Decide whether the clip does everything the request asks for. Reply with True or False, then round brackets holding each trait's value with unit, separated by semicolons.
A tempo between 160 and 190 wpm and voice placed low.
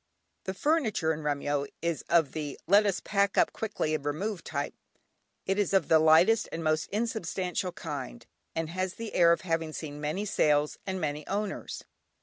False (175 wpm; 170 Hz)